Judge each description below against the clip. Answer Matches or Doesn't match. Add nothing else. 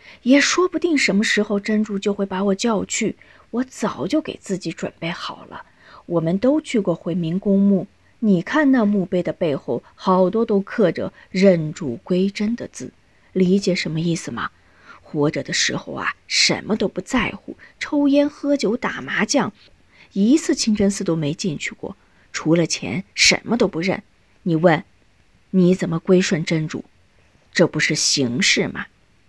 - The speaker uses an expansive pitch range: Doesn't match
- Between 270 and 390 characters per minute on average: Doesn't match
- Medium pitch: Doesn't match